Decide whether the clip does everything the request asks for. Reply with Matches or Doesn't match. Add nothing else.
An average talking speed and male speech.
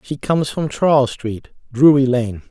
Matches